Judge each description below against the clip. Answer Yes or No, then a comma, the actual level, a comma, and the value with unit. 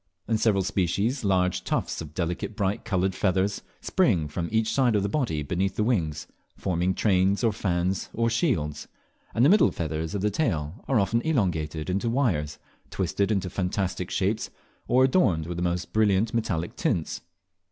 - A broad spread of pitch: No, average, 4.3 semitones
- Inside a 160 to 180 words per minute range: Yes, average, 170 wpm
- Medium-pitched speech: No, very low, 95 Hz